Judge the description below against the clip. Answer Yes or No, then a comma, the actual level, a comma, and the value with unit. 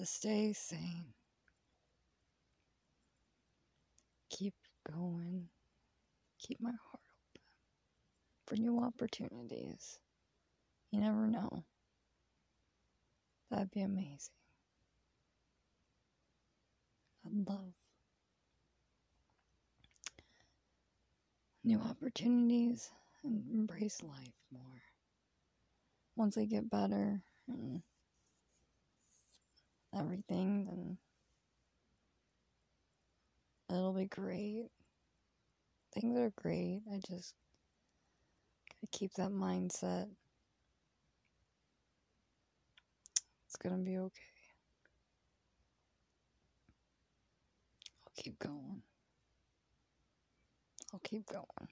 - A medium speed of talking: No, slow, 65 wpm